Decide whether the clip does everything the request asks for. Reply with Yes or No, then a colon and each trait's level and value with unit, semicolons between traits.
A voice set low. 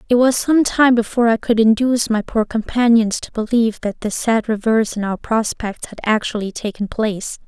No: high, 225 Hz